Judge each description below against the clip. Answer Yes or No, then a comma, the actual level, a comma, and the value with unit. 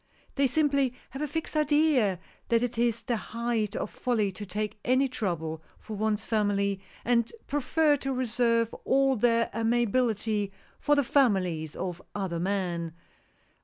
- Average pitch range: Yes, average, 4.3 semitones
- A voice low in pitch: No, high, 230 Hz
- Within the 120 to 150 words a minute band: Yes, average, 145 wpm